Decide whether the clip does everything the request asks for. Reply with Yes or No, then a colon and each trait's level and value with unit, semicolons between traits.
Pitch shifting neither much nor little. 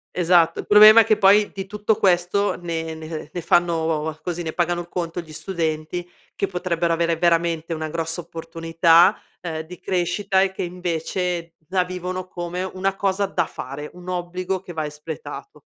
No: narrow, 2.1 semitones